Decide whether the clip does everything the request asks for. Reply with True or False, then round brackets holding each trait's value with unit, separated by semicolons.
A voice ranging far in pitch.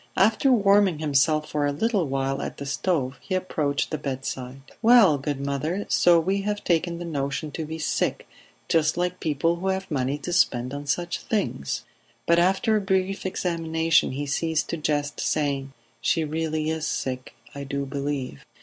False (4.2 semitones)